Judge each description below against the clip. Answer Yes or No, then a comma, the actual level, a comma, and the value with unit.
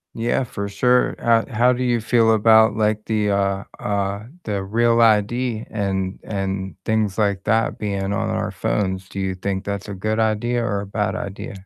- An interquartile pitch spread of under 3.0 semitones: Yes, narrow, 2.4 semitones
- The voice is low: Yes, low, 105 Hz